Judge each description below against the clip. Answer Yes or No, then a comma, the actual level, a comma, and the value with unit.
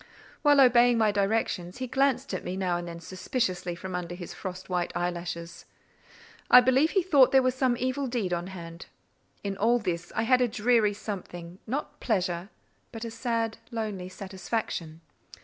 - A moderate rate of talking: Yes, average, 165 wpm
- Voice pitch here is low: No, high, 210 Hz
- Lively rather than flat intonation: Yes, wide, 5.7 semitones